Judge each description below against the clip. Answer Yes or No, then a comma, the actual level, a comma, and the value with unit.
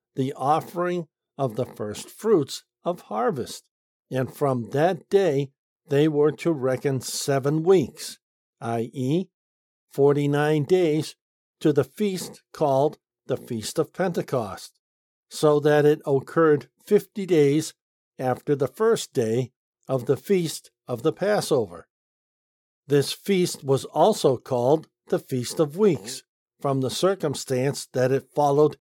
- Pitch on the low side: No, medium, 145 Hz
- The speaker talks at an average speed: No, slow, 125 wpm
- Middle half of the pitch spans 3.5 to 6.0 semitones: Yes, average, 4.1 semitones